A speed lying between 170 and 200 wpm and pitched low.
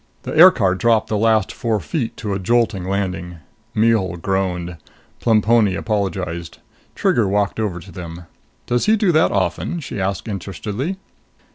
No: average, 145 wpm; low, 100 Hz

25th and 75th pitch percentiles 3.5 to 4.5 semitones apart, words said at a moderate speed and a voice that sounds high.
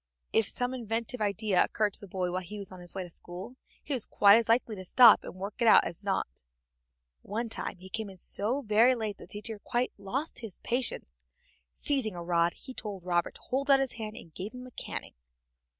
No: average, 4.2 semitones; fast, 230 wpm; high, 210 Hz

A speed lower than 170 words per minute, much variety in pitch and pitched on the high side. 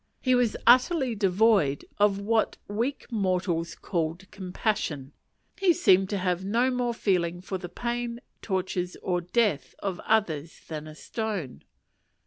No: slow, 135 wpm; average, 4.5 semitones; high, 195 Hz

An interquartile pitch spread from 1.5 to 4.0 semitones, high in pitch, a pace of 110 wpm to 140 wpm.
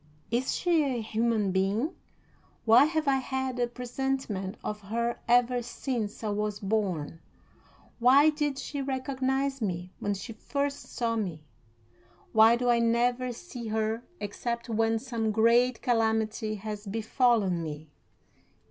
Yes: average, 3.2 semitones; high, 235 Hz; slow, 135 wpm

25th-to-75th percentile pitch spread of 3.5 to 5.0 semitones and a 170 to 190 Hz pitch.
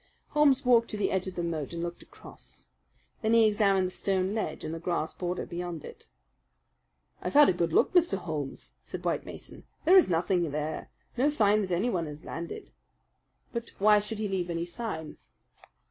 Yes: average, 4.6 semitones; medium, 185 Hz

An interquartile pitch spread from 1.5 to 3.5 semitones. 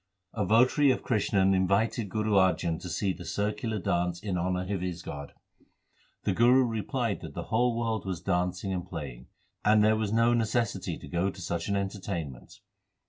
No: average, 4.0 semitones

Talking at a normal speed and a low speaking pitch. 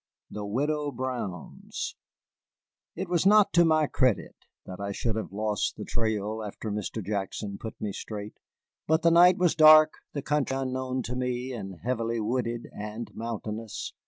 Yes: average, 160 wpm; low, 115 Hz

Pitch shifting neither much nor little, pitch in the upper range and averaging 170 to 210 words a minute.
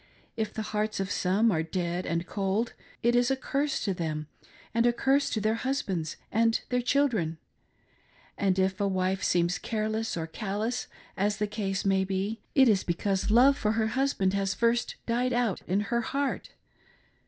Yes: average, 3.8 semitones; high, 210 Hz; average, 175 wpm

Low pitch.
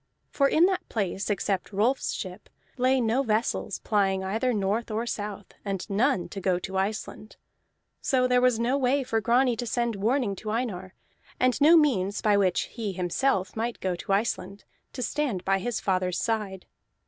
No: high, 220 Hz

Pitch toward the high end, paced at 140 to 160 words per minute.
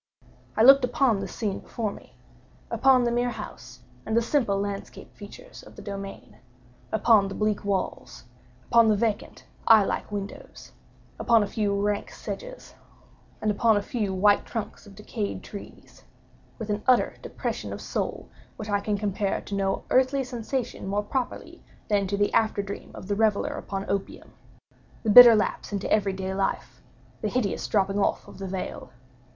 Yes: high, 210 Hz; average, 150 wpm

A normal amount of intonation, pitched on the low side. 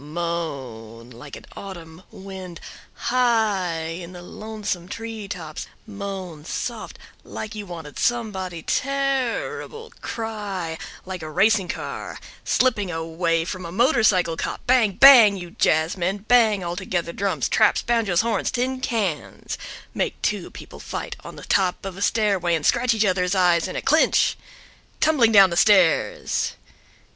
No: average, 4.6 semitones; high, 190 Hz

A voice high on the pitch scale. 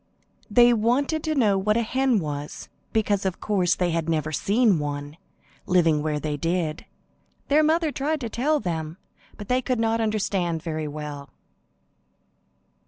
Yes: high, 195 Hz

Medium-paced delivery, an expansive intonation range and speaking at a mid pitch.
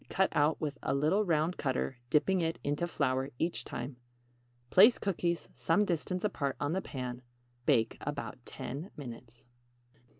No: average, 145 wpm; average, 4.8 semitones; medium, 150 Hz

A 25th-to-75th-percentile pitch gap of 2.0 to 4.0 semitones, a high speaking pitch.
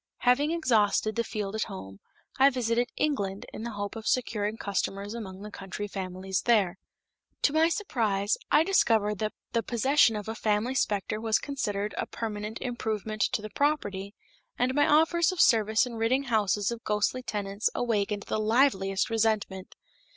Yes: average, 3.3 semitones; high, 220 Hz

